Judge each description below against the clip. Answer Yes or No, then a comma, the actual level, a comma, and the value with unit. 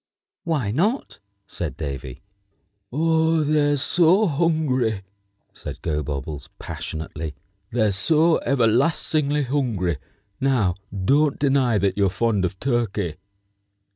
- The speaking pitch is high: No, low, 120 Hz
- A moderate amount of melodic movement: No, wide, 8.2 semitones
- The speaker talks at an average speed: No, slow, 100 wpm